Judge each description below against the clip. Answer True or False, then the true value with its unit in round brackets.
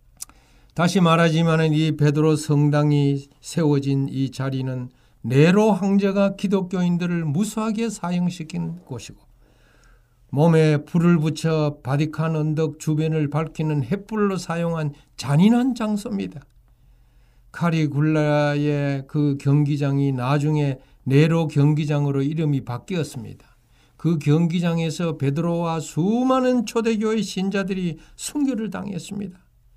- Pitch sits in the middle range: True (155 Hz)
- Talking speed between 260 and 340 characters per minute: True (265 characters per minute)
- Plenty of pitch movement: False (3.8 semitones)